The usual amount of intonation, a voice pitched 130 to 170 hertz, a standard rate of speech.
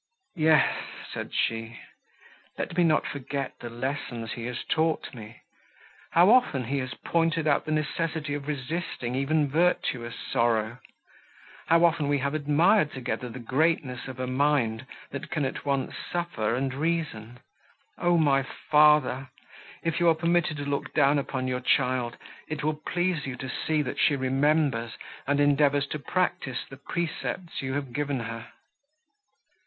Yes: average, 3.5 semitones; medium, 140 Hz; average, 155 wpm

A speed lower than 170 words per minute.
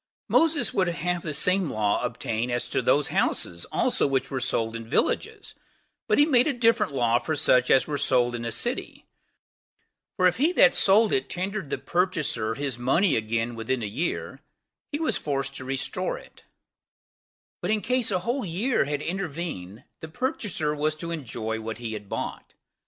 No: average, 180 wpm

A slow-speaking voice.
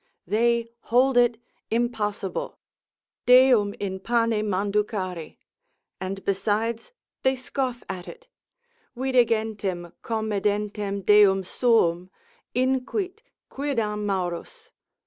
Yes: slow, 90 wpm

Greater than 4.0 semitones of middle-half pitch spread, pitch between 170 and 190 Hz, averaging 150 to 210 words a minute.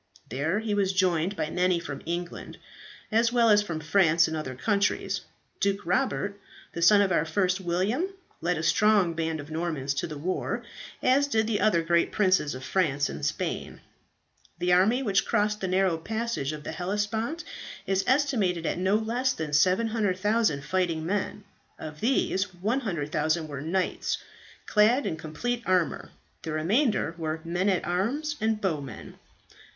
Yes: average, 4.6 semitones; medium, 185 Hz; average, 160 wpm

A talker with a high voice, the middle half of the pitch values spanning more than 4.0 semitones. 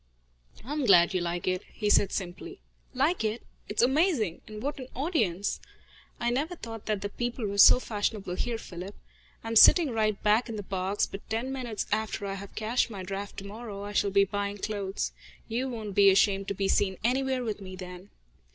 No: high, 210 Hz; average, 3.5 semitones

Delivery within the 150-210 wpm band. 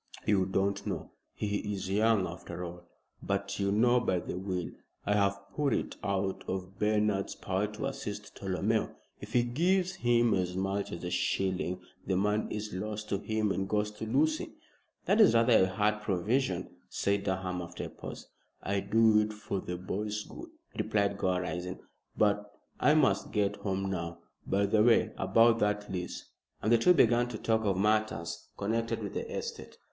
Yes: average, 180 wpm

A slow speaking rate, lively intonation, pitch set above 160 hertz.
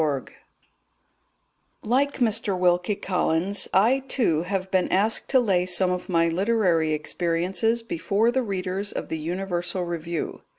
No: slow, 130 wpm; average, 3.6 semitones; medium, 185 Hz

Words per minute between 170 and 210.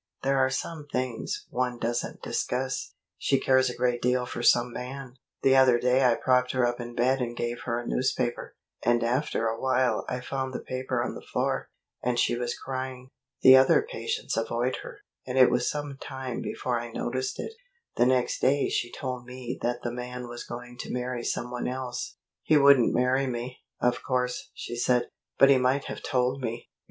Yes: average, 195 wpm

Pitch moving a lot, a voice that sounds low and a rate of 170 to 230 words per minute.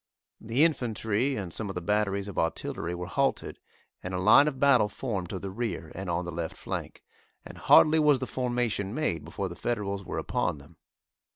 Yes: wide, 5.7 semitones; low, 105 Hz; average, 195 wpm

